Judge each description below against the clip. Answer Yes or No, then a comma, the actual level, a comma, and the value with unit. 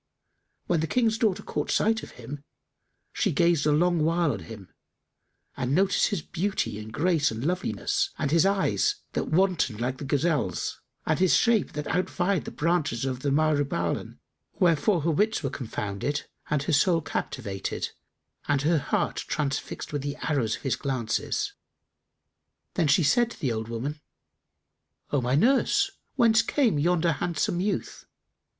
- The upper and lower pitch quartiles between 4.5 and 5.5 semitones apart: Yes, average, 5.2 semitones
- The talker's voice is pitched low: No, medium, 155 Hz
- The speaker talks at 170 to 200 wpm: No, average, 155 wpm